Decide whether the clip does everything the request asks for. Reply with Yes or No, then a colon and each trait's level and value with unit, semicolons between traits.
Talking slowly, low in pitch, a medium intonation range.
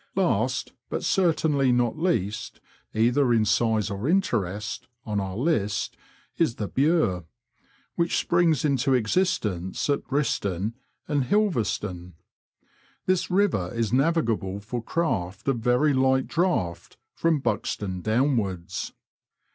No: slow, 115 wpm; low, 120 Hz; wide, 7.0 semitones